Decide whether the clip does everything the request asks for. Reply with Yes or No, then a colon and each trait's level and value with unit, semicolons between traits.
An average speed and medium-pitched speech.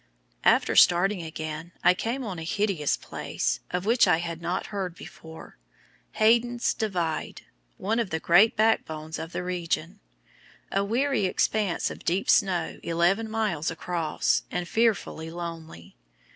Yes: average, 145 wpm; medium, 180 Hz